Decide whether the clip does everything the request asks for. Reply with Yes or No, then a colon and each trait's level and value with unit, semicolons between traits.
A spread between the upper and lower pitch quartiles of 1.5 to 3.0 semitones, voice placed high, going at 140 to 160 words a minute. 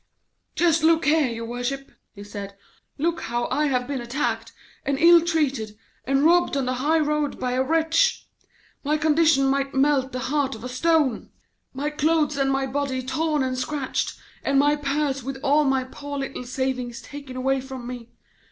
No: average, 2.7 semitones; very high, 275 Hz; average, 180 wpm